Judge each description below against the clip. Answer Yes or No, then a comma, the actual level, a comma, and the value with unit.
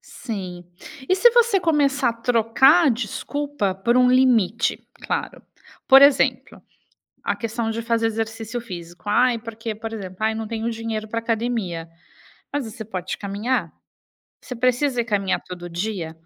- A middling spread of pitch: Yes, average, 3.2 semitones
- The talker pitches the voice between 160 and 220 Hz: No, high, 230 Hz